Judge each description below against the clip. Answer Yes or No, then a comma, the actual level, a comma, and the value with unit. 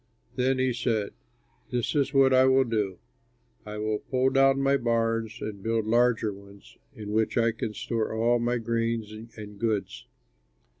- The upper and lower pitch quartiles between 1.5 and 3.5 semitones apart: Yes, average, 2.7 semitones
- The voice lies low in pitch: Yes, low, 115 Hz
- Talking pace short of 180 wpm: Yes, average, 160 wpm